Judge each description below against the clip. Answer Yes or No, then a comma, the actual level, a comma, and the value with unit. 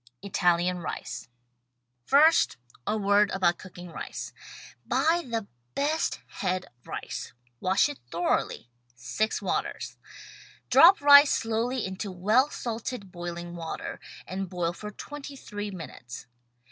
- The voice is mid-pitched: No, high, 200 Hz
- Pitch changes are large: Yes, wide, 6.1 semitones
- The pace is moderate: No, slow, 120 wpm